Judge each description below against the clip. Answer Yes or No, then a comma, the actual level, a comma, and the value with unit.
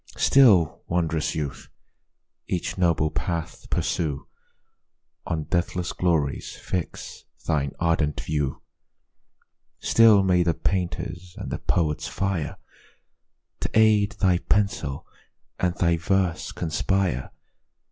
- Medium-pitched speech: No, very low, 85 Hz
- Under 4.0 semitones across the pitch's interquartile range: Yes, average, 3.2 semitones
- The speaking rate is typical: No, slow, 100 wpm